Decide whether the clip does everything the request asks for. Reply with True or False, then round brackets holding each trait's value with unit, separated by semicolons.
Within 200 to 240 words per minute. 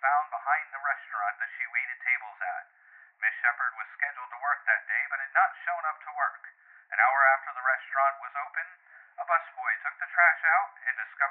True (205 wpm)